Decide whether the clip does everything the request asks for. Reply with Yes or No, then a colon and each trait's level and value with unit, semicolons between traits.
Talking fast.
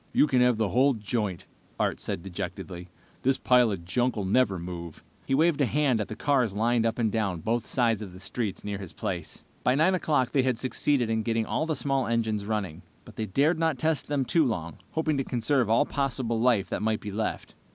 Yes: fast, 225 wpm